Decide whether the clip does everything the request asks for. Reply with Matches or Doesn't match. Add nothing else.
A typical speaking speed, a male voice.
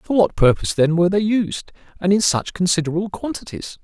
Matches